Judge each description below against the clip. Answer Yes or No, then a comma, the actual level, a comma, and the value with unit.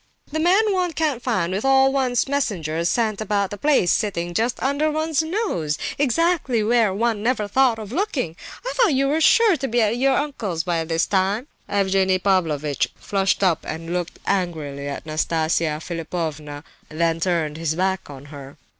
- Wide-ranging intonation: Yes, wide, 8.4 semitones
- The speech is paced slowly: No, average, 170 wpm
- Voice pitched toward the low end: No, high, 200 Hz